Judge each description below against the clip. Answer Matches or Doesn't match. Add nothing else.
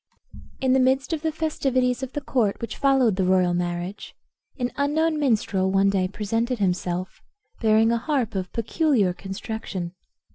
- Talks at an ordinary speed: Matches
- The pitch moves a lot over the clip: Matches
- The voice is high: Matches